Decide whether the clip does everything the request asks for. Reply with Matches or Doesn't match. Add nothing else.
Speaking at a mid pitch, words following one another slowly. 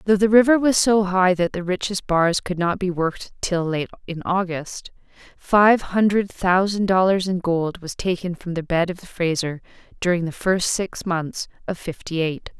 Doesn't match